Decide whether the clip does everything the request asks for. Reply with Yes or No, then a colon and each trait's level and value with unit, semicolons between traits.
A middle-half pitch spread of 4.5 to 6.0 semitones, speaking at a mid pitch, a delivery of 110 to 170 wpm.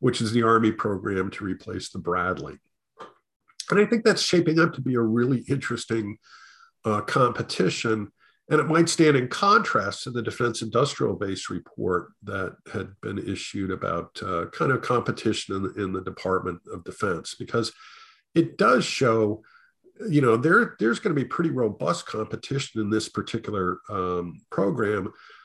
No: average, 5.2 semitones; low, 115 Hz; average, 165 wpm